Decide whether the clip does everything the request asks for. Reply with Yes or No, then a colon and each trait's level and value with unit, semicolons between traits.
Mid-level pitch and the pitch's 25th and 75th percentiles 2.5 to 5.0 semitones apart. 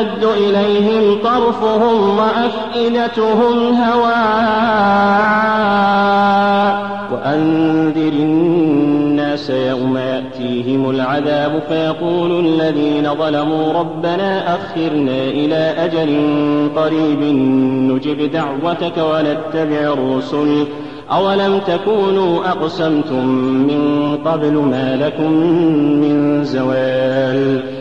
No: medium, 155 Hz; wide, 5.5 semitones